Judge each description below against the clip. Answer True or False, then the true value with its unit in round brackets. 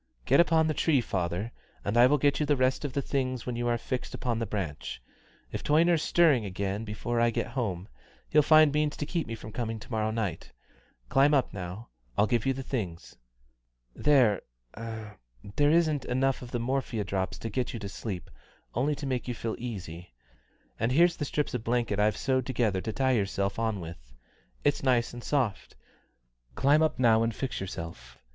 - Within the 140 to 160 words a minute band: False (195 wpm)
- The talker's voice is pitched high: False (120 Hz)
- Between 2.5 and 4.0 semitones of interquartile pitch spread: False (4.7 semitones)